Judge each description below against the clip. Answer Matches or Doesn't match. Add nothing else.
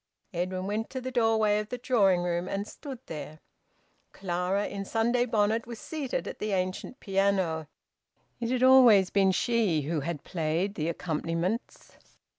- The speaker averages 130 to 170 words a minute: Matches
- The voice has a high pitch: Matches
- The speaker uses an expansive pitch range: Doesn't match